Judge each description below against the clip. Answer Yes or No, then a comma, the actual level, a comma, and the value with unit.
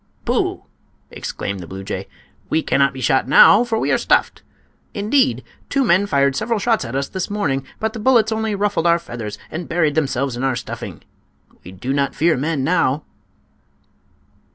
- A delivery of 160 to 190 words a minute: Yes, average, 175 wpm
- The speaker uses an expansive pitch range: Yes, wide, 7.6 semitones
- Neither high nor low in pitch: Yes, medium, 160 Hz